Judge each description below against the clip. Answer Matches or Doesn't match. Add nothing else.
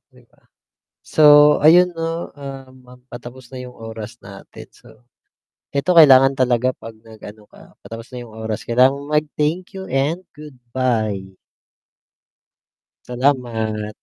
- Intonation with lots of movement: Doesn't match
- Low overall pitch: Matches